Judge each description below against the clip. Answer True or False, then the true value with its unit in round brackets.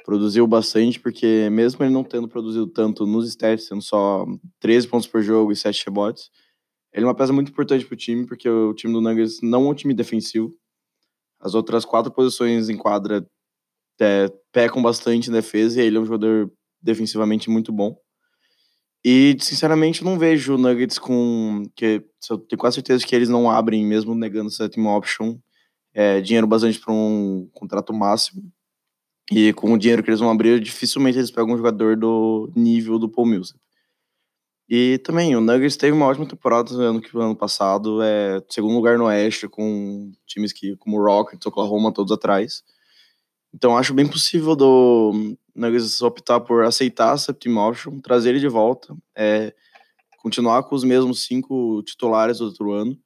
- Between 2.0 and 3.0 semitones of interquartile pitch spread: True (2.4 semitones)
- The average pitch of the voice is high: False (115 Hz)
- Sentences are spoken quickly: False (175 wpm)